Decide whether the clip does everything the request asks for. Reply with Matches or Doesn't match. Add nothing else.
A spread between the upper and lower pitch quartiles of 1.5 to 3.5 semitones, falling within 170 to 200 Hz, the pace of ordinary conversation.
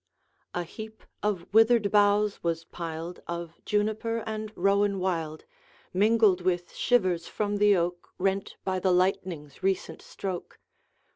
Doesn't match